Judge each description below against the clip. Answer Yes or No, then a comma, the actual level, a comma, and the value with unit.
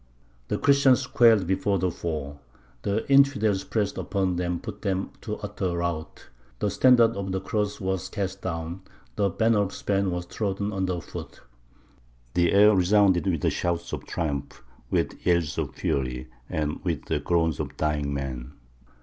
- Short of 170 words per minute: Yes, average, 160 wpm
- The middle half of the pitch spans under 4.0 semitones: Yes, average, 3.5 semitones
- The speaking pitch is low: Yes, very low, 95 Hz